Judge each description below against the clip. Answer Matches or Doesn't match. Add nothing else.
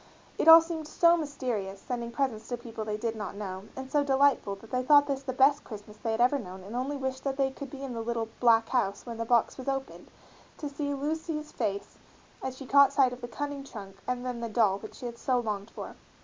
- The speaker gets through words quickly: Matches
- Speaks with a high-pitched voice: Matches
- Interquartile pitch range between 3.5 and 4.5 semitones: Matches